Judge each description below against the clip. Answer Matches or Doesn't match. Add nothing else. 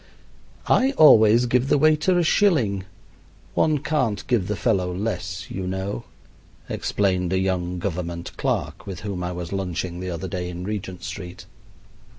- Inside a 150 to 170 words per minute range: Matches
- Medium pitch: Doesn't match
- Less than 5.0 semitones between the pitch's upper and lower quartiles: Matches